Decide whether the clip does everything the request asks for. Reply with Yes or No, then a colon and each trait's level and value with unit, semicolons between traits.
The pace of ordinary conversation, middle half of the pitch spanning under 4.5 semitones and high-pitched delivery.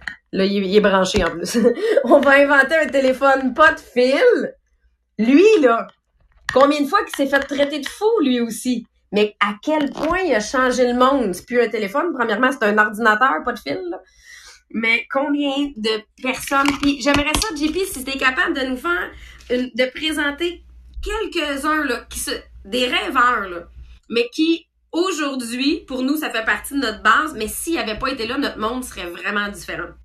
No: average, 190 wpm; average, 5.1 semitones; very high, 265 Hz